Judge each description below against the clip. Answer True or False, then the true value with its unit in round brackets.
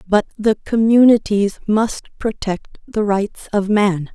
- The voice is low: False (210 Hz)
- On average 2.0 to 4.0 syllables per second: True (3.6 syllables/s)